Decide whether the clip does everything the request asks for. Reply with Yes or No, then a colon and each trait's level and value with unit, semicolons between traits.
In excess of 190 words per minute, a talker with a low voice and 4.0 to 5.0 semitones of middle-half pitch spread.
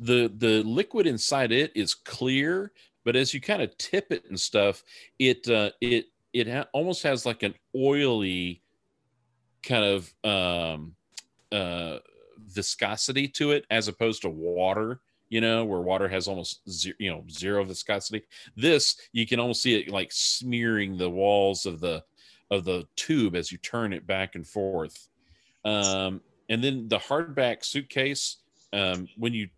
No: average, 160 wpm; low, 110 Hz; average, 4.3 semitones